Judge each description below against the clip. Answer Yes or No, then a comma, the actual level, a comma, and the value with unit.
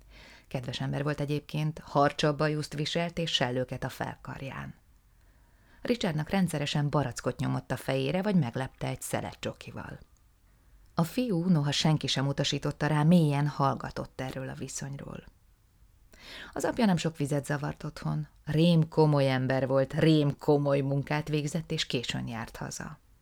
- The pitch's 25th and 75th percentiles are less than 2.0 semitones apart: No, narrow, 2.6 semitones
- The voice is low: No, medium, 150 Hz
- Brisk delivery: No, average, 135 wpm